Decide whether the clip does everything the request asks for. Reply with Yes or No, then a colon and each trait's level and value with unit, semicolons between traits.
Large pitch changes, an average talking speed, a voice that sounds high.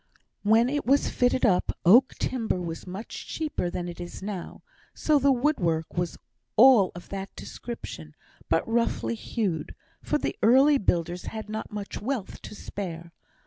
Yes: wide, 6.0 semitones; average, 160 wpm; high, 210 Hz